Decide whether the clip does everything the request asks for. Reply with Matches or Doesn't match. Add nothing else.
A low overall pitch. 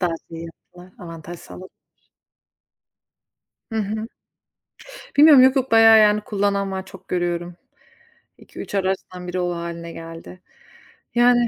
Doesn't match